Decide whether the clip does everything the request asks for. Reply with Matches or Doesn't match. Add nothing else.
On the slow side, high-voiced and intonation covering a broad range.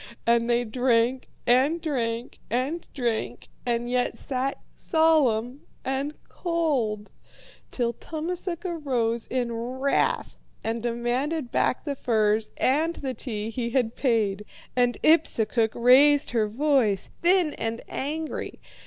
Doesn't match